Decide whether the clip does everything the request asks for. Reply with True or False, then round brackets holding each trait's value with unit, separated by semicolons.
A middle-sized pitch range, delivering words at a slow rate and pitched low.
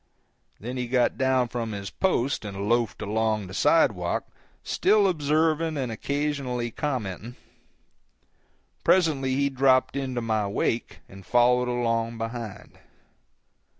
True (3.8 semitones; 115 wpm; 125 Hz)